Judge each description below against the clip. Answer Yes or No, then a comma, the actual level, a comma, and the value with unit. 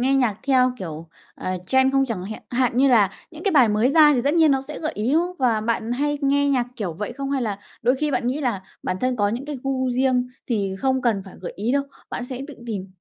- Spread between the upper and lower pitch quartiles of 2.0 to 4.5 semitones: Yes, average, 3.9 semitones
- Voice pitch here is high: Yes, very high, 255 Hz